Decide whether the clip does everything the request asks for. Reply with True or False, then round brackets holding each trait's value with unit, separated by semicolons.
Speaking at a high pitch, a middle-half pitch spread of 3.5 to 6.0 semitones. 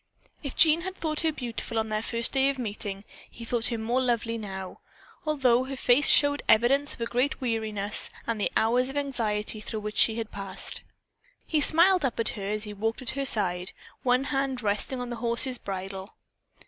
True (235 Hz; 4.1 semitones)